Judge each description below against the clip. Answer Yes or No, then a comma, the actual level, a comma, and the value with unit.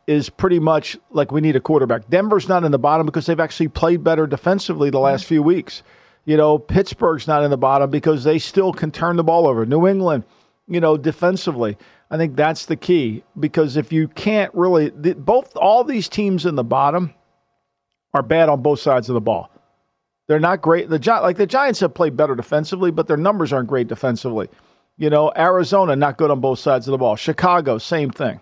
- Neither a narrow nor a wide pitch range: Yes, average, 3.4 semitones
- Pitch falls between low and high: Yes, medium, 160 Hz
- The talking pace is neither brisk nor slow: No, fast, 215 wpm